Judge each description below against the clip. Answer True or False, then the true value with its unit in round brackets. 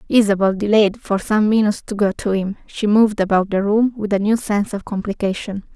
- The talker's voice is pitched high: True (205 Hz)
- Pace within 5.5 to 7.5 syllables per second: True (5.7 syllables/s)